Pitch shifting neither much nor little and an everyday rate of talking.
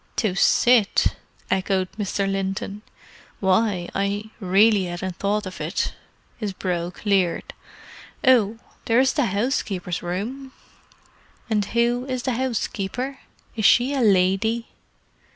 No: average, 3.8 semitones; slow, 115 wpm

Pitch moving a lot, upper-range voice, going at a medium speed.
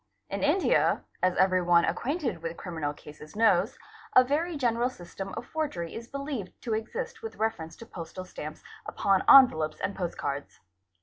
Yes: wide, 7.0 semitones; high, 200 Hz; average, 160 wpm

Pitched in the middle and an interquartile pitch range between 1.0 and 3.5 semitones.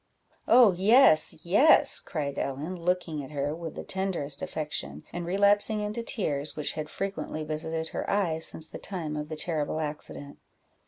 No: medium, 160 Hz; average, 4.3 semitones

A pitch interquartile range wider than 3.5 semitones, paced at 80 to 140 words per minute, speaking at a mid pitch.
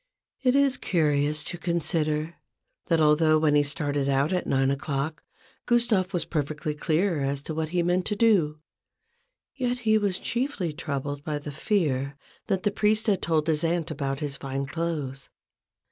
No: average, 4.2 semitones; average, 165 wpm; medium, 155 Hz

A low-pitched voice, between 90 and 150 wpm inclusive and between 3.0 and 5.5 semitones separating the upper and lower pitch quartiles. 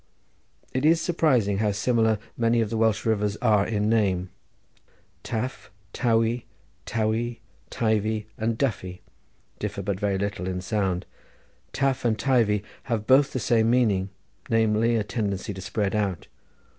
No: low, 110 Hz; average, 140 wpm; narrow, 2.5 semitones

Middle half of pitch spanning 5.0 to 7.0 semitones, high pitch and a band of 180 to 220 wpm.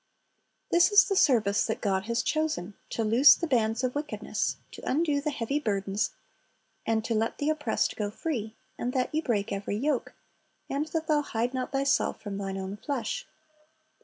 Yes: wide, 5.5 semitones; high, 245 Hz; average, 190 wpm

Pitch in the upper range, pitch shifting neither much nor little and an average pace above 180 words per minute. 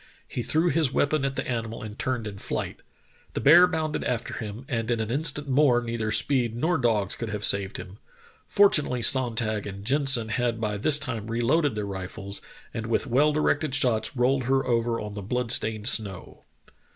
No: low, 120 Hz; average, 4.1 semitones; average, 190 wpm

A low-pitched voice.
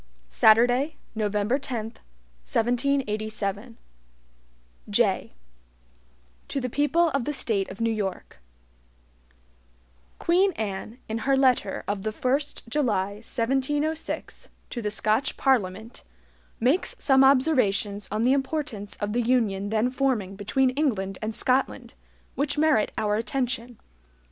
No: high, 235 Hz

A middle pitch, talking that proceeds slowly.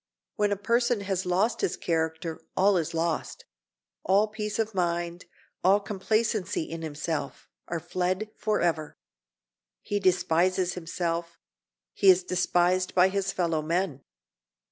Yes: medium, 180 Hz; slow, 120 wpm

